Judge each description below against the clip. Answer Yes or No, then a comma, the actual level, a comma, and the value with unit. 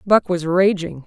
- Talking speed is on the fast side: No, average, 170 wpm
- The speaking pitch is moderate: Yes, medium, 180 Hz